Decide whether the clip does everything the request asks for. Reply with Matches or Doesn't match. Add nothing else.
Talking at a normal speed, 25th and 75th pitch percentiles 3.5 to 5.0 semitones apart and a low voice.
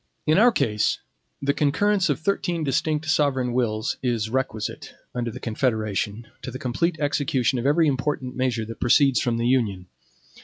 Matches